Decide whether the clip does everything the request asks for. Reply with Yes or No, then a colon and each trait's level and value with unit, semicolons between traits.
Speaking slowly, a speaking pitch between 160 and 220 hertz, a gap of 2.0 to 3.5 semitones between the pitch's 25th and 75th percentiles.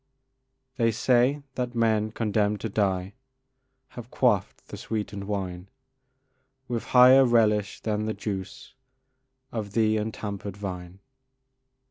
No: slow, 110 wpm; low, 110 Hz; average, 2.7 semitones